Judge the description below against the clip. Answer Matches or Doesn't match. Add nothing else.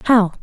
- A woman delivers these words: Matches